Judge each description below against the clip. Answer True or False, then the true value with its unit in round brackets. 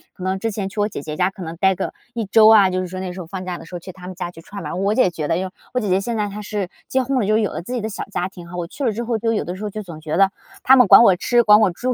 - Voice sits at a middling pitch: False (195 Hz)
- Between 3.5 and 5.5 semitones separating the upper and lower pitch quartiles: False (3.1 semitones)